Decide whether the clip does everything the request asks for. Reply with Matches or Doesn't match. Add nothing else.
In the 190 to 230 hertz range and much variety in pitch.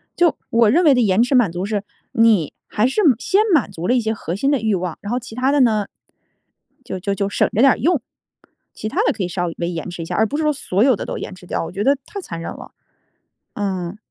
Matches